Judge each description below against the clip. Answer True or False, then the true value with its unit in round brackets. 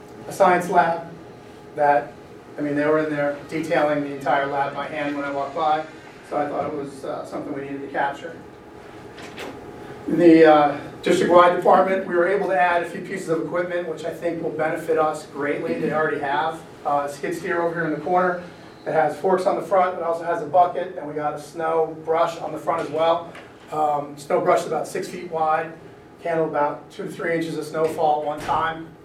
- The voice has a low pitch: False (160 Hz)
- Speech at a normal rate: False (220 wpm)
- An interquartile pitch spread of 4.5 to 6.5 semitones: False (2.5 semitones)